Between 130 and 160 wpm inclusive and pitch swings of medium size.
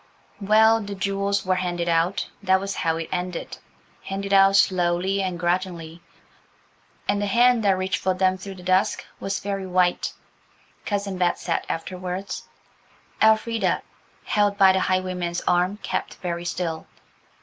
No: average, 140 wpm; narrow, 1.9 semitones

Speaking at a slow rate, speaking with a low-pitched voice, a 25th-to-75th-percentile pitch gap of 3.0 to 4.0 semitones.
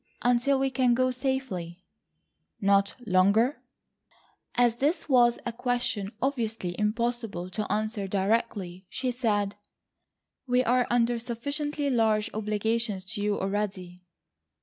No: slow, 115 wpm; high, 230 Hz; average, 3.6 semitones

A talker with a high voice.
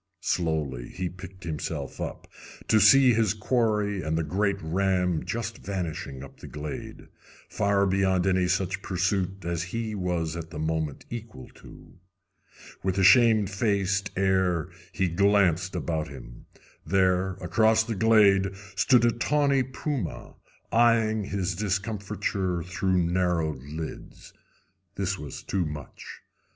No: very low, 95 Hz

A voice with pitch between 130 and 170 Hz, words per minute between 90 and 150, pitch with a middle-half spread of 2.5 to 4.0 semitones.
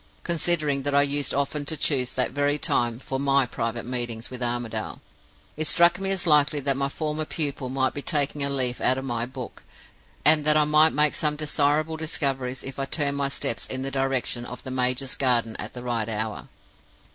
No: medium, 140 Hz; fast, 205 wpm; average, 3.0 semitones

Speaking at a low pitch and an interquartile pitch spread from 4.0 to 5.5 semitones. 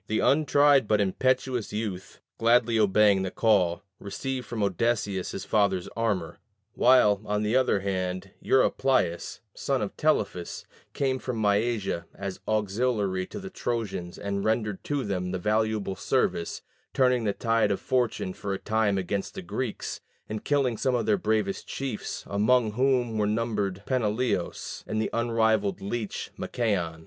No: low, 110 Hz; average, 3.6 semitones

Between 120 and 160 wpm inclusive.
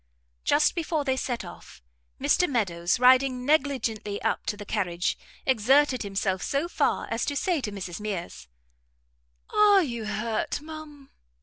Yes: average, 140 wpm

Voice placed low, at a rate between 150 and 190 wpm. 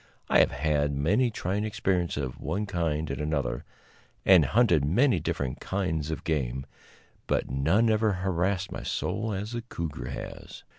Yes: very low, 85 Hz; average, 155 wpm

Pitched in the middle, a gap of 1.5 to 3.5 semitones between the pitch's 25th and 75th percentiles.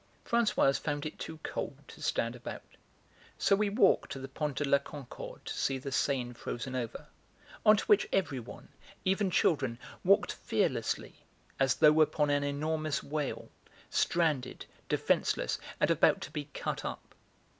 Yes: medium, 145 Hz; average, 3.1 semitones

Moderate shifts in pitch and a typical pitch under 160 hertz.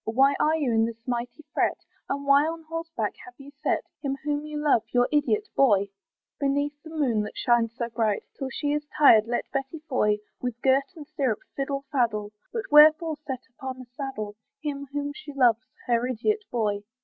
No: average, 3.9 semitones; very high, 275 Hz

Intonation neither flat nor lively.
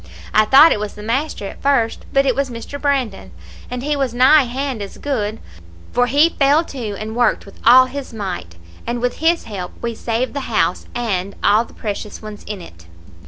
Yes: average, 4.6 semitones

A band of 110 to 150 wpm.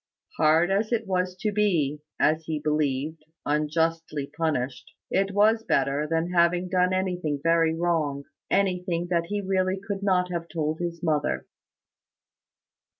Yes: average, 140 wpm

